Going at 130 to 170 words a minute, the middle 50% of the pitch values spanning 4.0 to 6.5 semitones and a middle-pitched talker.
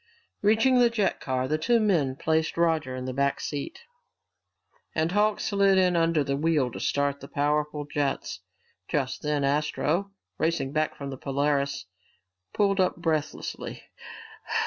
Yes: average, 145 wpm; average, 4.3 semitones; medium, 150 Hz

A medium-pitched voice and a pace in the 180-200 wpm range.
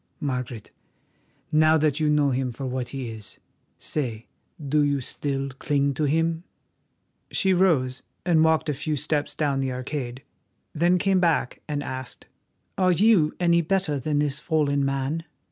No: medium, 145 Hz; average, 155 wpm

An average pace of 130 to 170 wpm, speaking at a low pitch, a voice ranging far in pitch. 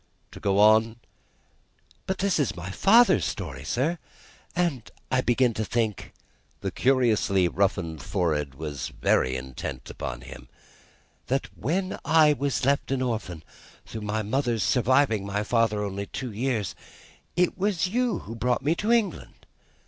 Yes: average, 150 wpm; low, 115 Hz; wide, 6.2 semitones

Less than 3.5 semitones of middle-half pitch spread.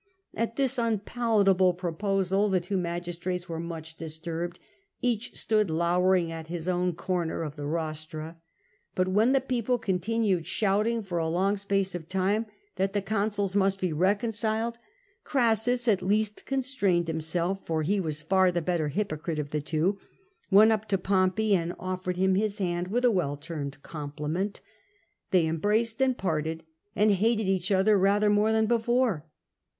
No: average, 4.0 semitones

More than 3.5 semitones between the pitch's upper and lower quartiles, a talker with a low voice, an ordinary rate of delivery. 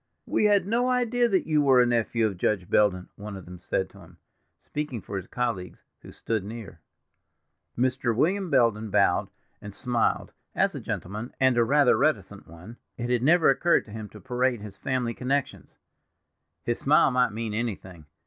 Yes: average, 4.7 semitones; low, 120 Hz; average, 180 wpm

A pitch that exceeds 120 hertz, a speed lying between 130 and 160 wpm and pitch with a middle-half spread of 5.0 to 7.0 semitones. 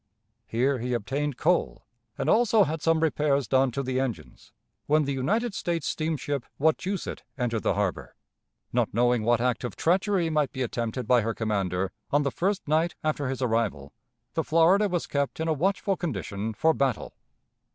No: medium, 140 Hz; average, 170 wpm; average, 5.3 semitones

